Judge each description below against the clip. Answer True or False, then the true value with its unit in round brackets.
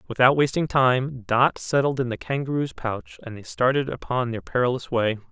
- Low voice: True (125 Hz)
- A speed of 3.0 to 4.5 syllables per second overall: False (5.0 syllables/s)